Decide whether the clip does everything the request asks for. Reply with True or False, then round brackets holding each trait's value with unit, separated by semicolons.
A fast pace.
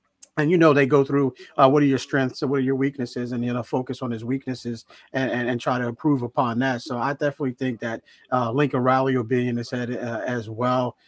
True (255 wpm)